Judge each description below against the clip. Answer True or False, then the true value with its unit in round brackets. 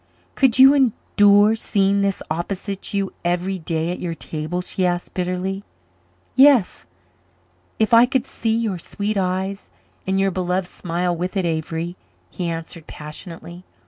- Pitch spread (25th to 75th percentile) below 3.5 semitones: True (2.7 semitones)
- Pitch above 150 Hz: True (185 Hz)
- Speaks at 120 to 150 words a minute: True (145 wpm)